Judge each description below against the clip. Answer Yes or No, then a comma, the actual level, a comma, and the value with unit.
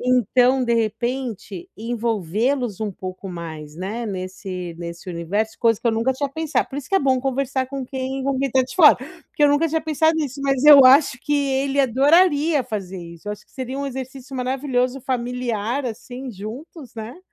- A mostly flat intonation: No, average, 4.2 semitones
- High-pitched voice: Yes, very high, 250 Hz